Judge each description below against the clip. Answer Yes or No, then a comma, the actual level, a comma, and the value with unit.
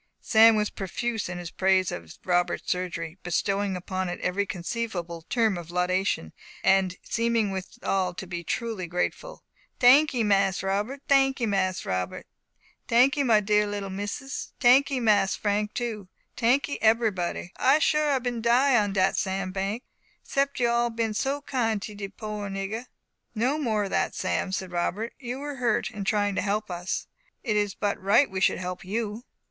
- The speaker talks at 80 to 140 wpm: No, average, 170 wpm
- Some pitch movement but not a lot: Yes, average, 4.0 semitones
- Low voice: No, high, 210 Hz